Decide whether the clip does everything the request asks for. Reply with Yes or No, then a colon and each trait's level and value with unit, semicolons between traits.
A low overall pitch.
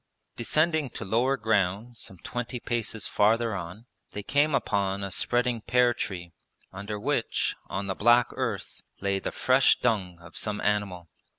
Yes: low, 110 Hz